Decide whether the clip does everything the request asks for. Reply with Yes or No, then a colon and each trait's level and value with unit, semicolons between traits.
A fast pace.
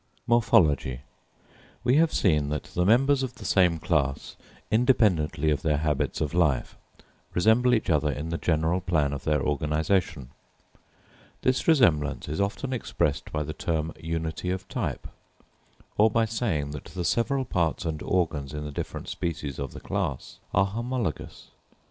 No: average, 155 wpm